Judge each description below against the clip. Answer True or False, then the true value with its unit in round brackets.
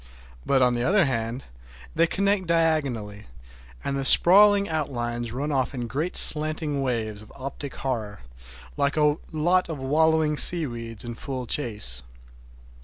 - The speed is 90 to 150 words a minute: True (140 wpm)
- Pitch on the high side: False (140 Hz)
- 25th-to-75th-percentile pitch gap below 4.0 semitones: False (5.0 semitones)